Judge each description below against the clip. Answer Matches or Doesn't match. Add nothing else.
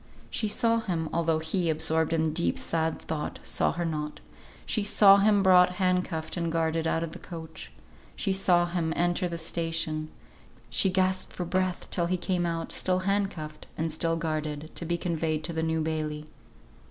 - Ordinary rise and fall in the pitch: Doesn't match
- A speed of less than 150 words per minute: Doesn't match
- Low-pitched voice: Doesn't match